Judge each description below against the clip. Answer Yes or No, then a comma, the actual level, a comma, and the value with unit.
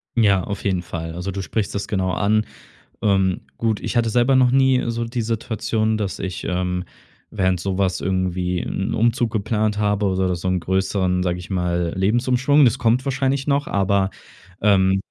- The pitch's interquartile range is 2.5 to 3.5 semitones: No, average, 3.9 semitones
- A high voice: No, low, 100 Hz